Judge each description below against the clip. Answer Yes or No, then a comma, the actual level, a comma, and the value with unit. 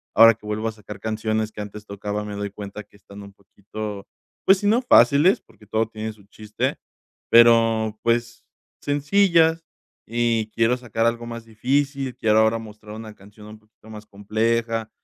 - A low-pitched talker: Yes, low, 110 Hz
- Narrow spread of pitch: Yes, narrow, 1.8 semitones